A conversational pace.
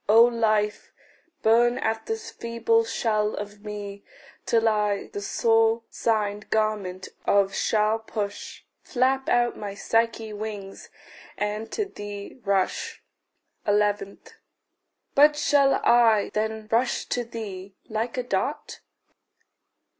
No: slow, 115 wpm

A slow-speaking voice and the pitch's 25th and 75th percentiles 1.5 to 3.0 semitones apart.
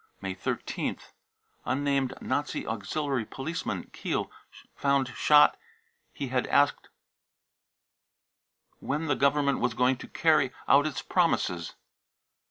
Yes: slow, 105 wpm; average, 2.7 semitones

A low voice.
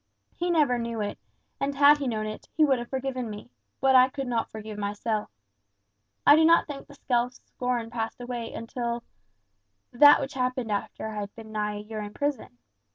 No: high, 240 Hz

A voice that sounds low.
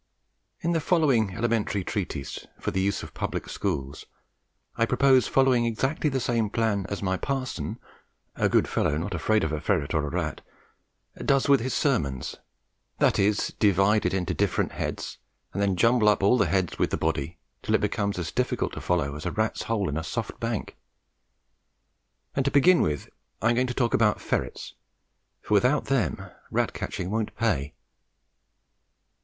Yes: low, 105 Hz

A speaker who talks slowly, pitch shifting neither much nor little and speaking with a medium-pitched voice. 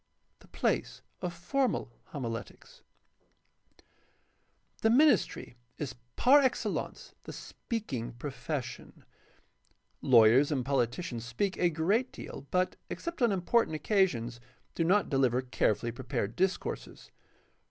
No: slow, 110 wpm; wide, 8.6 semitones; medium, 150 Hz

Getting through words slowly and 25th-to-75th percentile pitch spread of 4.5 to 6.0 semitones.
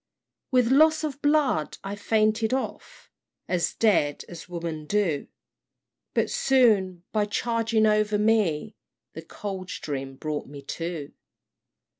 Yes: slow, 115 wpm; wide, 5.5 semitones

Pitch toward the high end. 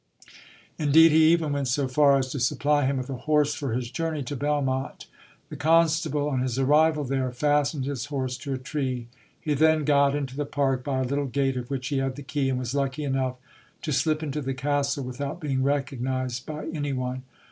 No: medium, 140 Hz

